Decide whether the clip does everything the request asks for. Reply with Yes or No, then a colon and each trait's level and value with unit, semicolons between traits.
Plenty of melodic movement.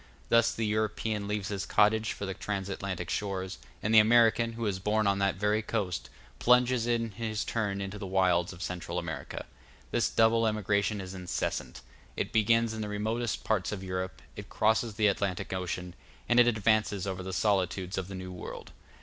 No: average, 2.7 semitones